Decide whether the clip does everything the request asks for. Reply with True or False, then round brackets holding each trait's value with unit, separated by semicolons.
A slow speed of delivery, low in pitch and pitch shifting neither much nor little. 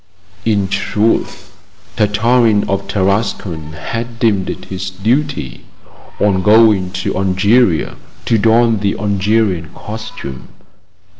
True (100 wpm; 105 Hz; 3.0 semitones)